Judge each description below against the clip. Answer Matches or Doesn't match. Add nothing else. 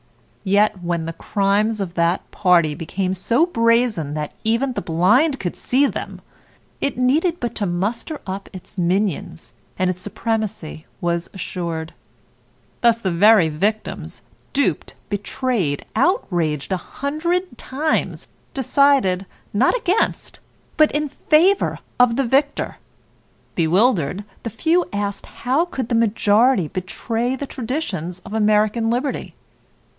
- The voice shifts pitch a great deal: Matches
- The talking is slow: Matches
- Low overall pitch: Doesn't match